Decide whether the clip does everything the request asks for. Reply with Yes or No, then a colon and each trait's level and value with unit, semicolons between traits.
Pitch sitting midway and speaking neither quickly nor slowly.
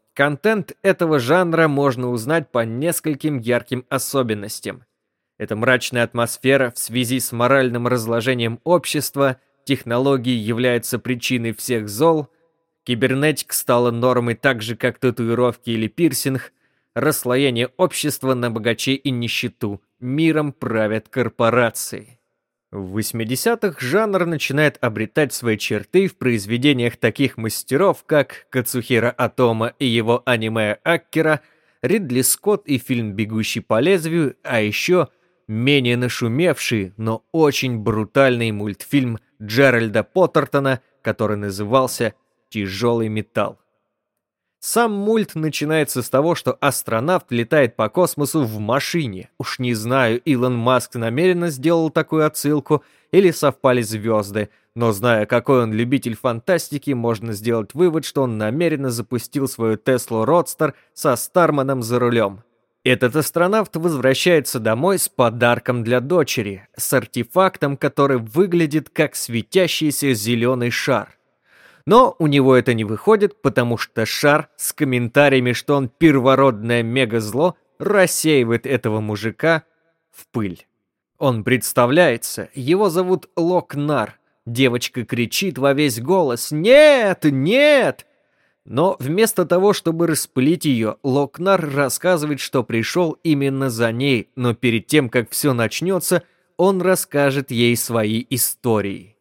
No: low, 130 Hz; average, 120 wpm